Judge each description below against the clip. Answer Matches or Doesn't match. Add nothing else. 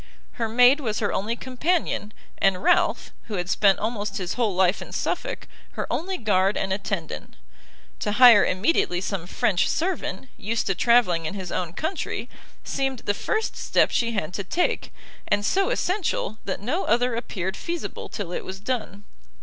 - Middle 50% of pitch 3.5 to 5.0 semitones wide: Matches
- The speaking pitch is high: Matches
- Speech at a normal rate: Matches